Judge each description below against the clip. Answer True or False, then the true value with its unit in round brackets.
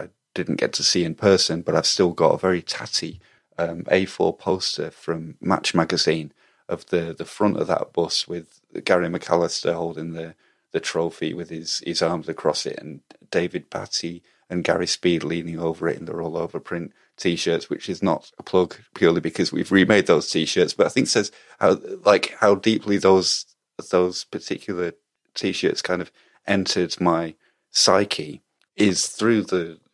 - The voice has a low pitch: True (85 Hz)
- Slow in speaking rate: False (175 wpm)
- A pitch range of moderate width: False (2.1 semitones)